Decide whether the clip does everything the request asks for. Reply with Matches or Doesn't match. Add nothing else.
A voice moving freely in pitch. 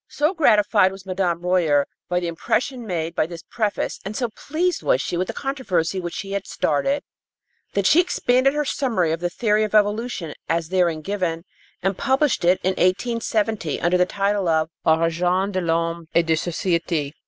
Doesn't match